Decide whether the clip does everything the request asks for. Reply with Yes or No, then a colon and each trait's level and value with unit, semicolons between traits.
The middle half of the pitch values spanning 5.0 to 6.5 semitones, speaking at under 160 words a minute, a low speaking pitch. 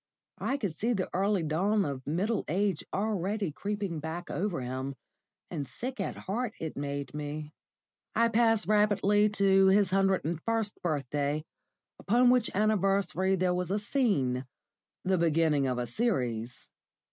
No: wide, 5.6 semitones; average, 145 wpm; high, 190 Hz